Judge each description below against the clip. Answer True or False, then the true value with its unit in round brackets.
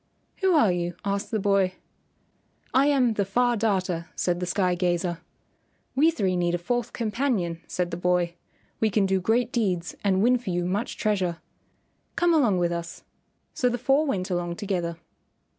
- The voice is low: False (195 Hz)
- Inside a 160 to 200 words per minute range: True (175 wpm)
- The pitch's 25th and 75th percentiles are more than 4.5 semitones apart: True (5.1 semitones)